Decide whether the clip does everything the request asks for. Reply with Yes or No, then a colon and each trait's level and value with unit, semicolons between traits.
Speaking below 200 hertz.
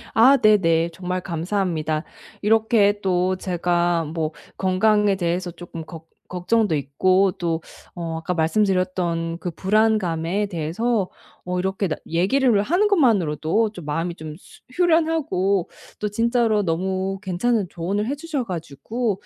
Yes: medium, 185 Hz